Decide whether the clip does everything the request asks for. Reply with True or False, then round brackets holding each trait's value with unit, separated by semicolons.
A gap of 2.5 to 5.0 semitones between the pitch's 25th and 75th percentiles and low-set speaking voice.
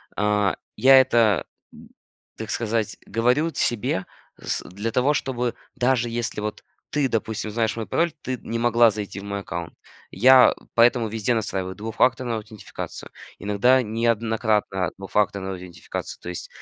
True (2.8 semitones; 110 Hz)